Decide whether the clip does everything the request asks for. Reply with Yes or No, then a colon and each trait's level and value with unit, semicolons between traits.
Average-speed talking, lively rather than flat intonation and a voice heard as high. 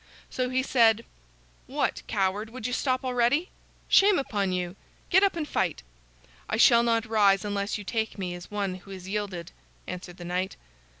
No: average, 175 wpm; average, 4.7 semitones; high, 210 Hz